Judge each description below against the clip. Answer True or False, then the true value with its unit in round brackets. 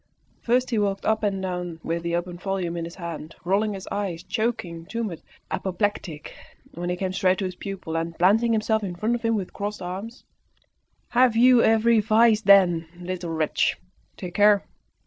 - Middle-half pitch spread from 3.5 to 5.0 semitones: True (3.9 semitones)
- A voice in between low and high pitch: False (195 Hz)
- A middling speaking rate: True (180 wpm)